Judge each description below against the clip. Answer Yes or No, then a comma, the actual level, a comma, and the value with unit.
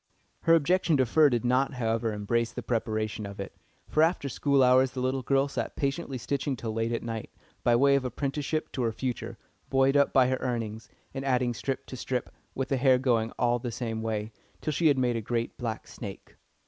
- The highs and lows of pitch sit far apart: No, average, 3.0 semitones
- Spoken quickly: Yes, fast, 210 wpm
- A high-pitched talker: No, low, 125 Hz